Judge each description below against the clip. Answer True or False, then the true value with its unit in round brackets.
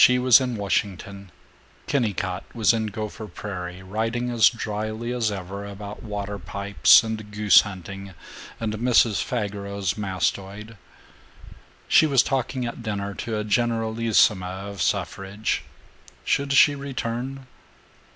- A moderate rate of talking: False (125 wpm)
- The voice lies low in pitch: True (105 Hz)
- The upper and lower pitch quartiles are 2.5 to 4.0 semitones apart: True (2.8 semitones)